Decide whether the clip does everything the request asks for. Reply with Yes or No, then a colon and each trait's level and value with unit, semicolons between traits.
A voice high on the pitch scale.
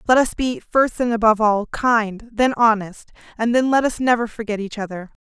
Yes: high, 225 Hz